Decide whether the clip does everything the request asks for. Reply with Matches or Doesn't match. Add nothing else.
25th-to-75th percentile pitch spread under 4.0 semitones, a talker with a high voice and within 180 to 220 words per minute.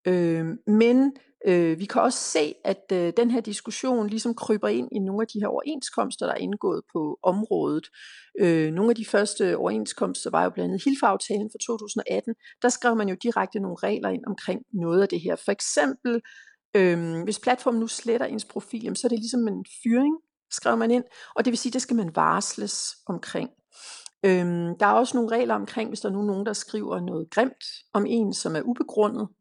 Matches